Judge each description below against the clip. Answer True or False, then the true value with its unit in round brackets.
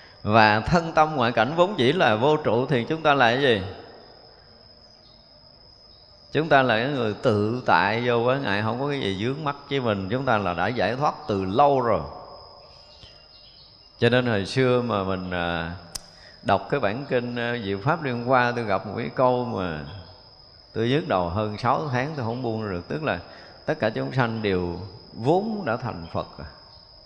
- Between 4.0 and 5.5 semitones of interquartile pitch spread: True (4.8 semitones)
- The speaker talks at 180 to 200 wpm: True (190 wpm)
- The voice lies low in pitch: True (115 Hz)